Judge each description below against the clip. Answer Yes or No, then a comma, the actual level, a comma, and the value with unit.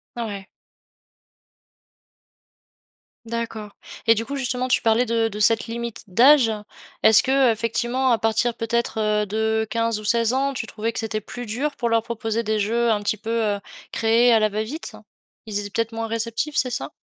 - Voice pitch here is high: Yes, high, 230 Hz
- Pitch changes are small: Yes, narrow, 1.5 semitones